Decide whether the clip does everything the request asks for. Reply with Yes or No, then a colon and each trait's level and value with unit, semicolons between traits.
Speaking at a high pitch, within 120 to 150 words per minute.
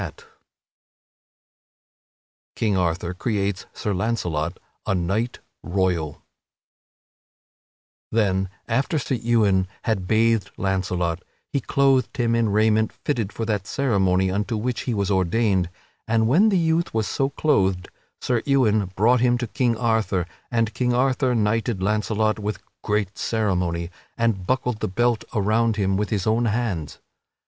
No: low, 110 Hz; slow, 135 wpm